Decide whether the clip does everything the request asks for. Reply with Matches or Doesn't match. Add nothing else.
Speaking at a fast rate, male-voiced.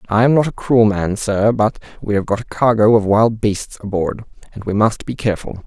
Matches